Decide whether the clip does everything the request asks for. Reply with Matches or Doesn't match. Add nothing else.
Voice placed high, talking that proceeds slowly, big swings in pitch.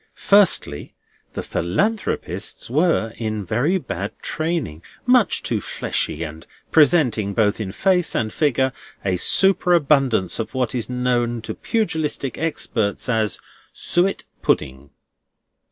Doesn't match